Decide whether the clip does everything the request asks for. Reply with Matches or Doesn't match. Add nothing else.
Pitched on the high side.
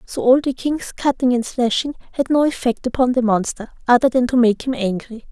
Matches